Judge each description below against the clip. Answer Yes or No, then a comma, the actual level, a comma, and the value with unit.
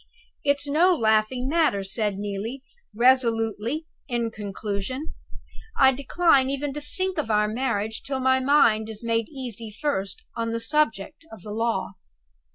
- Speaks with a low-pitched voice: No, high, 235 Hz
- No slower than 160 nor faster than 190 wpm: No, average, 145 wpm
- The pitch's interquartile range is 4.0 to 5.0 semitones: Yes, average, 4.5 semitones